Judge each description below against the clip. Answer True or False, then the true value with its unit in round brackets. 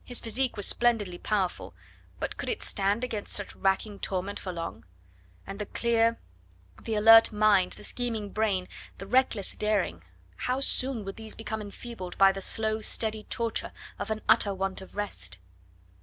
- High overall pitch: True (210 Hz)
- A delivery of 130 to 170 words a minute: True (165 wpm)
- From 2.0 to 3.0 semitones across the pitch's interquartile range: True (2.7 semitones)